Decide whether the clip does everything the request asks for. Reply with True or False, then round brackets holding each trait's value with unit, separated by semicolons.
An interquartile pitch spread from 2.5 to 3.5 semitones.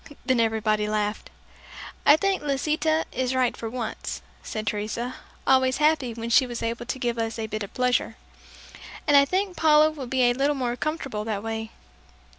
False (4.2 semitones)